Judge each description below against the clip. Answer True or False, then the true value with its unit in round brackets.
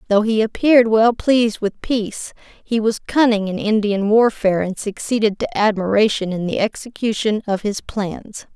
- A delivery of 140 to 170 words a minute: True (160 wpm)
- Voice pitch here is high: True (215 Hz)